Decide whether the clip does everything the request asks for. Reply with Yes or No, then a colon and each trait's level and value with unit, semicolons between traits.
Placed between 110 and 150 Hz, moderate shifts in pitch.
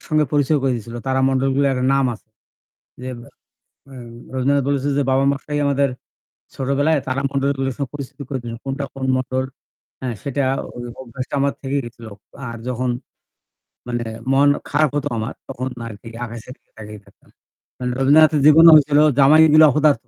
No: low, 135 Hz; narrow, 1.9 semitones